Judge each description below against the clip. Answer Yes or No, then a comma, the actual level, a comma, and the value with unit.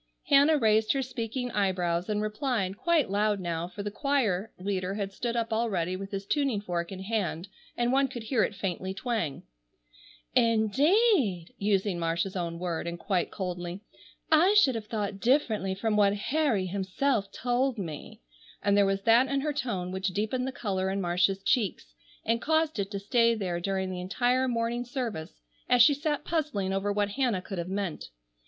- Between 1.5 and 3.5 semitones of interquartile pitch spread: No, average, 4.6 semitones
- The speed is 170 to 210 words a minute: Yes, average, 175 wpm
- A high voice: Yes, high, 205 Hz